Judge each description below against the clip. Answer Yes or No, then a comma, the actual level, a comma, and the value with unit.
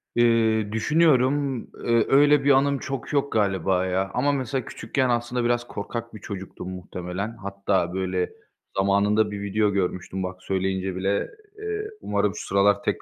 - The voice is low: Yes, low, 105 Hz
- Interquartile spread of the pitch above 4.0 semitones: Yes, average, 4.7 semitones